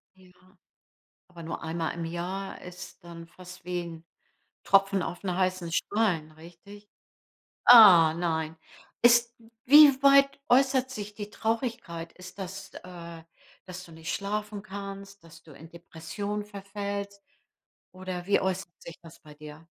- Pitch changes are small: No, average, 3.5 semitones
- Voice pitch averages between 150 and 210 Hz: Yes, medium, 185 Hz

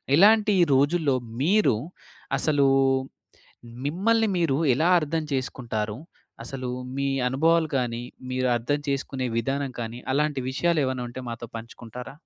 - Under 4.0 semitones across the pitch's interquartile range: No, average, 4.3 semitones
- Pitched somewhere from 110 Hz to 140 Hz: Yes, low, 135 Hz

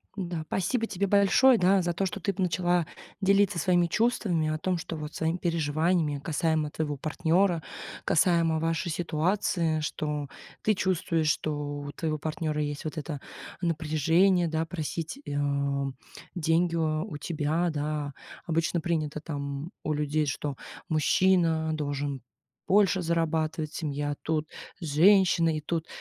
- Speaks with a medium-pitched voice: Yes, medium, 160 Hz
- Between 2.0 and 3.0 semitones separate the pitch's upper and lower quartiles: Yes, average, 2.7 semitones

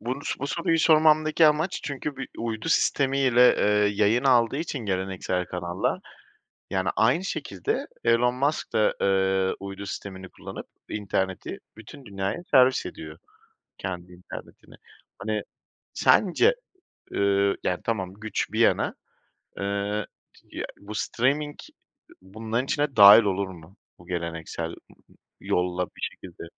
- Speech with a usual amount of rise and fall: No, wide, 6.0 semitones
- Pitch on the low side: Yes, low, 105 Hz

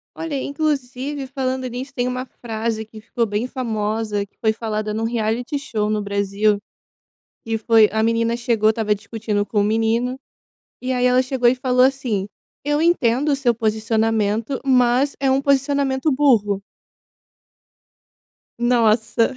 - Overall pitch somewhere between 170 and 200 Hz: No, high, 235 Hz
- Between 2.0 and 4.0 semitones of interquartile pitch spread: Yes, average, 3.1 semitones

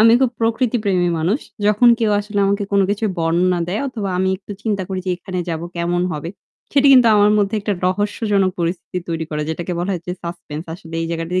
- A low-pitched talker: No, high, 190 Hz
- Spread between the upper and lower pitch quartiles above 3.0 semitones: Yes, average, 3.5 semitones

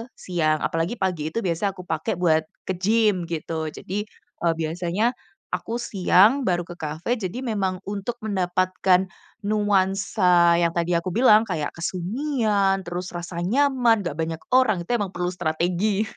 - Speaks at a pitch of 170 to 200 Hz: Yes, medium, 185 Hz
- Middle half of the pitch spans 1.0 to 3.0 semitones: No, average, 3.7 semitones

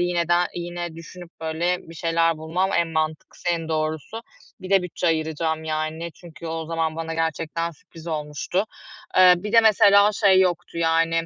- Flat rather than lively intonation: Yes, narrow, 1.7 semitones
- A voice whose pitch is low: No, medium, 165 Hz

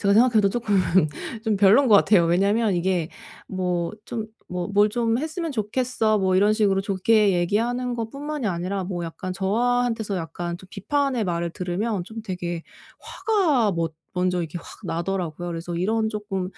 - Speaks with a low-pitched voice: No, high, 200 Hz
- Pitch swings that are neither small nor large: Yes, average, 4.0 semitones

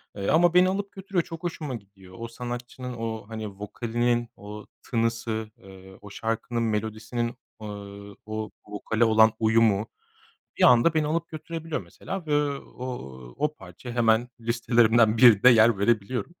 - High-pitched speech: No, low, 115 Hz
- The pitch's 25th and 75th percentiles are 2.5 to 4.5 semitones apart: Yes, average, 2.8 semitones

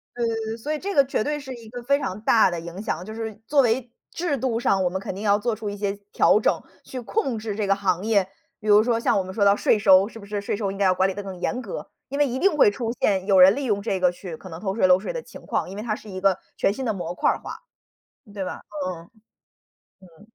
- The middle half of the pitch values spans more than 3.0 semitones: Yes, average, 3.7 semitones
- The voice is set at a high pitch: Yes, high, 210 Hz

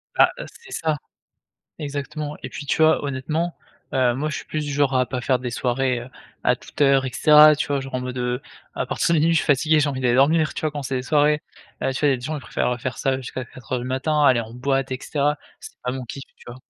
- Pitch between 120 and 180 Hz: Yes, low, 135 Hz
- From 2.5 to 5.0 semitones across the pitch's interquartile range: Yes, average, 2.9 semitones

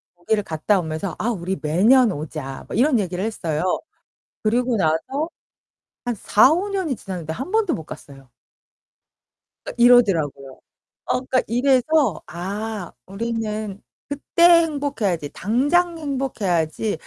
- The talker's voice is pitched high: Yes, high, 215 Hz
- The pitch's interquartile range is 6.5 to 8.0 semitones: Yes, wide, 7.6 semitones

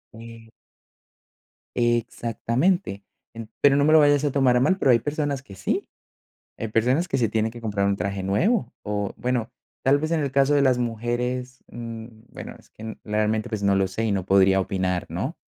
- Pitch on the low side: Yes, low, 115 Hz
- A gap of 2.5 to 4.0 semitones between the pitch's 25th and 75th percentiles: No, average, 4.6 semitones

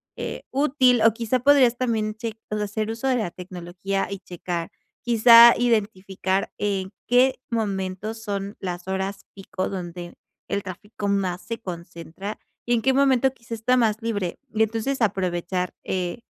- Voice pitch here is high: Yes, high, 210 Hz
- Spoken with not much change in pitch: No, average, 3.7 semitones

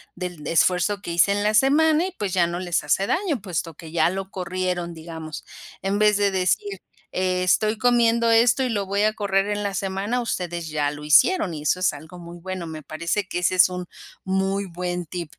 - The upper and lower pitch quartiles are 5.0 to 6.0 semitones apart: No, average, 3.2 semitones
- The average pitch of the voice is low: No, medium, 185 Hz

